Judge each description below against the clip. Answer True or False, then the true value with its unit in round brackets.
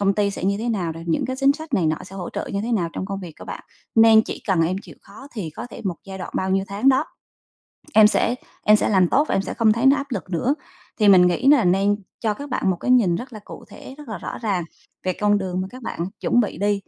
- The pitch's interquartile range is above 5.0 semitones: False (4.3 semitones)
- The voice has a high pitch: True (205 Hz)